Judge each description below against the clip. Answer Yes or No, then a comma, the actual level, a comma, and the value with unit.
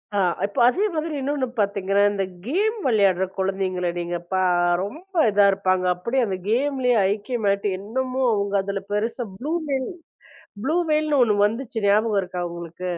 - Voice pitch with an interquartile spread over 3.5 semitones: Yes, average, 5.3 semitones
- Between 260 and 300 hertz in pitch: No, high, 205 Hz